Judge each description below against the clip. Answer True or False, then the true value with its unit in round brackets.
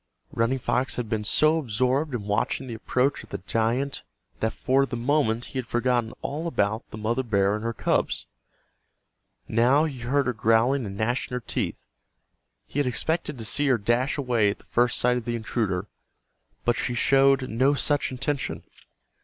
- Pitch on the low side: True (125 Hz)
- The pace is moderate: True (180 wpm)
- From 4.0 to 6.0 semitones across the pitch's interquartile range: False (3.2 semitones)